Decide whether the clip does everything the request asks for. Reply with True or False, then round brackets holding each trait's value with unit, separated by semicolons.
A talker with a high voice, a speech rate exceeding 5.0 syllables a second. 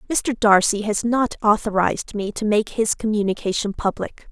False (215 Hz; 4.9 syllables/s)